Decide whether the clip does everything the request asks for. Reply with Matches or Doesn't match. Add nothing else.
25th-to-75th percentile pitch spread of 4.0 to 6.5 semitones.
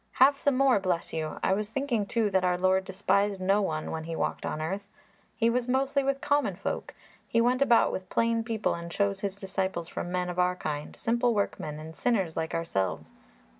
Matches